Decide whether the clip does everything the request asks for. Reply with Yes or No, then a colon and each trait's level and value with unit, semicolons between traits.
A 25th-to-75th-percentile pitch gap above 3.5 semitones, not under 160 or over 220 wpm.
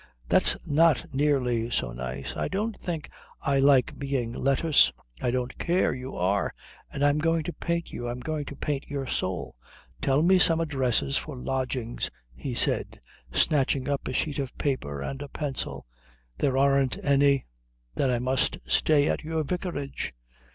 No: average, 3.1 semitones; average, 165 wpm